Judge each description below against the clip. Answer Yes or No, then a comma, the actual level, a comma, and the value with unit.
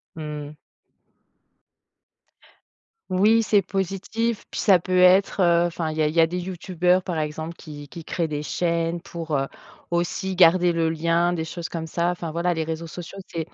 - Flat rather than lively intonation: Yes, narrow, 2.1 semitones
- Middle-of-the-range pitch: Yes, medium, 170 Hz